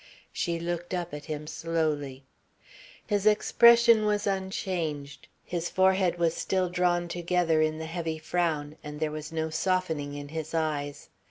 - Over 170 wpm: No, average, 150 wpm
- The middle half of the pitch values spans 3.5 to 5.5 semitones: No, average, 2.9 semitones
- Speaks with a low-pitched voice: No, medium, 165 Hz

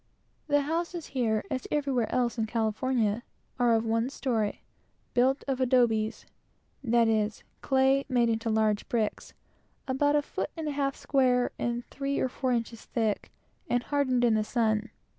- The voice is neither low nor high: No, high, 245 Hz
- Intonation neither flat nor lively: Yes, average, 3.4 semitones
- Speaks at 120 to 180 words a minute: Yes, average, 145 wpm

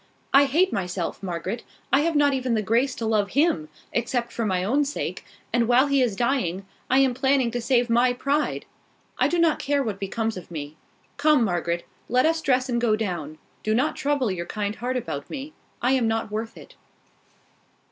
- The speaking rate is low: No, average, 200 wpm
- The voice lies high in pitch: Yes, high, 240 Hz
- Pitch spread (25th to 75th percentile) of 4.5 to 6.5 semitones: Yes, average, 5.0 semitones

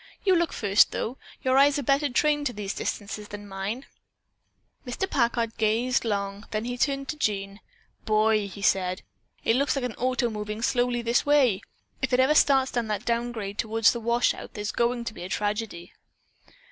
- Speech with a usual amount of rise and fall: Yes, average, 3.7 semitones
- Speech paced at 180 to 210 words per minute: Yes, average, 190 wpm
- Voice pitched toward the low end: No, high, 235 Hz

